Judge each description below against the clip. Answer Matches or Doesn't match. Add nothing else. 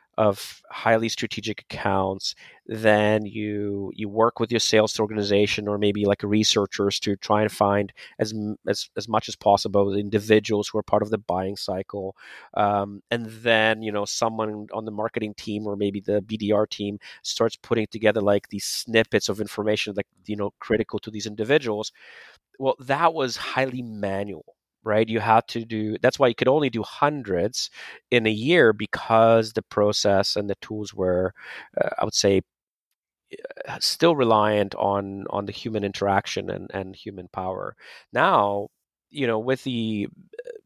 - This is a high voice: Doesn't match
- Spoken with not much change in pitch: Matches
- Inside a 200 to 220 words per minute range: Doesn't match